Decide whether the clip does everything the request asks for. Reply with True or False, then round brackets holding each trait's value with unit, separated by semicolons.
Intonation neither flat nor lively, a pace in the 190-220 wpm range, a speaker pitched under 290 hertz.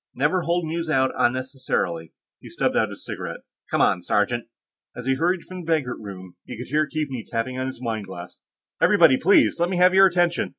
False (6.4 semitones; 205 wpm; 135 Hz)